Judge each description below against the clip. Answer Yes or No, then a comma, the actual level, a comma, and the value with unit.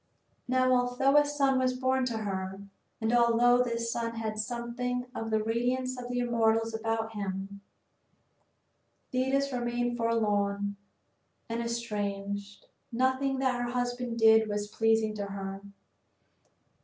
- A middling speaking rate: No, slow, 130 wpm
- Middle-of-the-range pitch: No, high, 235 Hz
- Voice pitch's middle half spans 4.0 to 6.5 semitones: No, narrow, 2.5 semitones